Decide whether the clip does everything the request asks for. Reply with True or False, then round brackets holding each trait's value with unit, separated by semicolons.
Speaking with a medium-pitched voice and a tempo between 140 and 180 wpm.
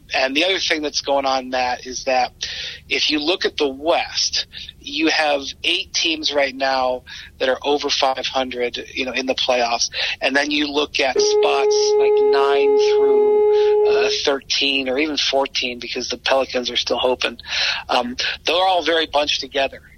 True (145 Hz; 175 wpm)